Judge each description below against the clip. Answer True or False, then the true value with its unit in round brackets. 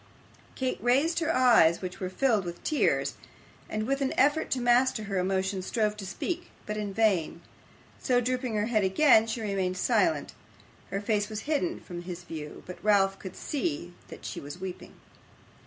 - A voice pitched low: False (215 Hz)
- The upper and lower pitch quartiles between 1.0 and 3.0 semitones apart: False (5.2 semitones)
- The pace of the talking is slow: False (175 wpm)